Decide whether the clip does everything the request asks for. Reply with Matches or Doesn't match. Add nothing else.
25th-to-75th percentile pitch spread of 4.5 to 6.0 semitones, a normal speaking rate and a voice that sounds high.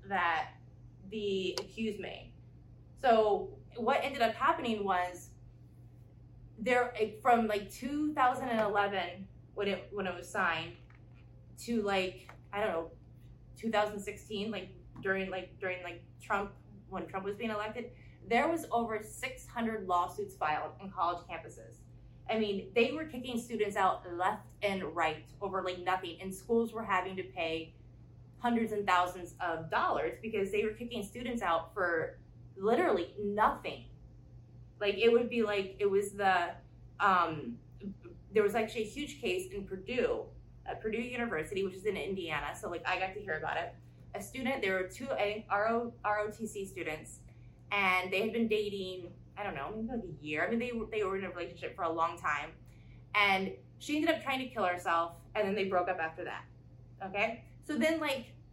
Matches